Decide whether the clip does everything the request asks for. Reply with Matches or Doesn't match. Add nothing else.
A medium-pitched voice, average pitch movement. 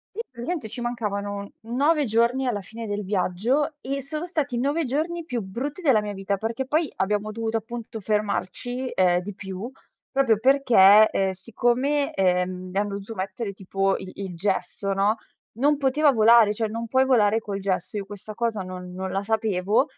Doesn't match